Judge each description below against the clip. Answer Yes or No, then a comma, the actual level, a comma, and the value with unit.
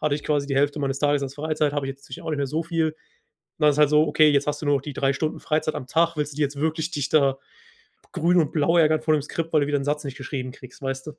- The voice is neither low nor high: Yes, medium, 150 Hz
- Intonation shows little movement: Yes, narrow, 1.9 semitones